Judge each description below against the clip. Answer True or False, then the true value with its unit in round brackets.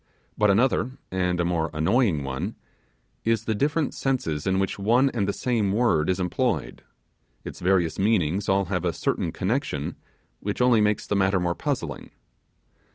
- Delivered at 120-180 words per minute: True (160 wpm)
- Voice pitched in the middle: False (95 Hz)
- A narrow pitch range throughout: False (4.5 semitones)